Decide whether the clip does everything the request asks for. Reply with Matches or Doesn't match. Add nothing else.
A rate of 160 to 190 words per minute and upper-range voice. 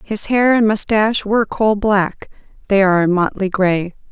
Matches